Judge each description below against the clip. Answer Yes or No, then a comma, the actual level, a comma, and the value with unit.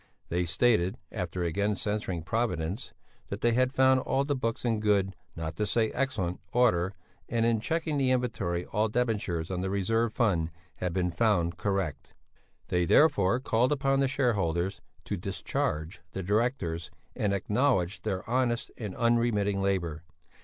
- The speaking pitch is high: No, low, 105 Hz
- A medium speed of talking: Yes, average, 155 wpm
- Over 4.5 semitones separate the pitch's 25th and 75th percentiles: Yes, average, 5.2 semitones